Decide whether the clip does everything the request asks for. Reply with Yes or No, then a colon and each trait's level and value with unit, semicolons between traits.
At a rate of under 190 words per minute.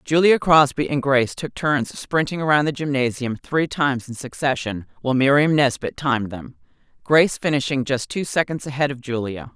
Yes: average, 170 wpm